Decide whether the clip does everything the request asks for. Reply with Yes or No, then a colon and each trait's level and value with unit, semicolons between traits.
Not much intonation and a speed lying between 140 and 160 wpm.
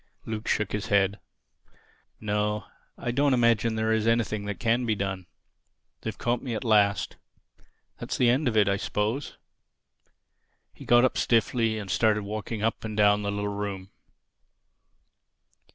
Yes: narrow, 2.2 semitones; average, 150 wpm